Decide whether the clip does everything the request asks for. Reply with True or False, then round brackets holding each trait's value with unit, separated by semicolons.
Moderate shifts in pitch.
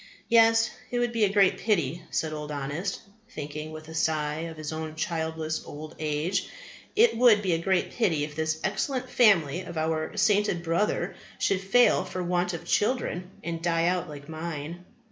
True (4.1 semitones)